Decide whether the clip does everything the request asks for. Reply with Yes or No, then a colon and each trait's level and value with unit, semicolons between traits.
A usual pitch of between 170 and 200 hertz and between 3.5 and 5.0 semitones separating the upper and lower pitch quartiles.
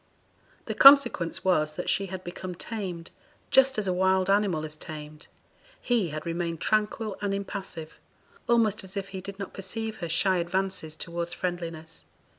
No: medium, 185 Hz; average, 3.0 semitones